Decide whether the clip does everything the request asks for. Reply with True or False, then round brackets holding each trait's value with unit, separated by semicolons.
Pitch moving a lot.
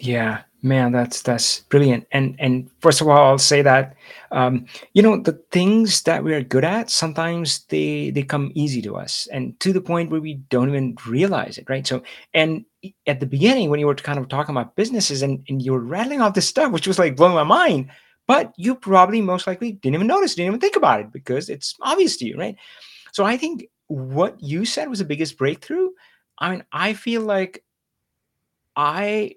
True (7.2 semitones)